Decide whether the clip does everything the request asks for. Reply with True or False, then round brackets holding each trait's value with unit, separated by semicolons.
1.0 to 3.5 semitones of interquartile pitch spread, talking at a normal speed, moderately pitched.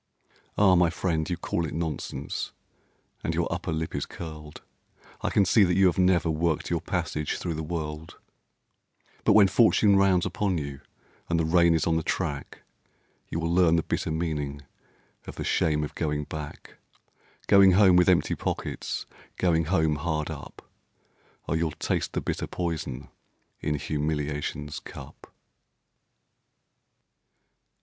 False (2.8 semitones; 150 wpm; 80 Hz)